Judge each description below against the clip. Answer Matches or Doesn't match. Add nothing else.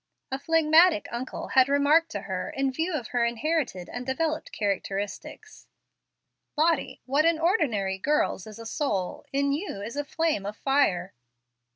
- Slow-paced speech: Doesn't match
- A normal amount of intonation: Doesn't match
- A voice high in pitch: Matches